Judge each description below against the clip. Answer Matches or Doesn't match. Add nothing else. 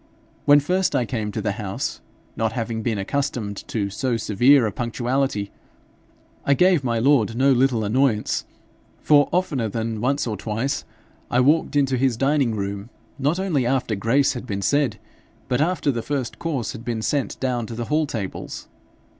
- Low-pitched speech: Matches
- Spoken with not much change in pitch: Doesn't match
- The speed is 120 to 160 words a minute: Doesn't match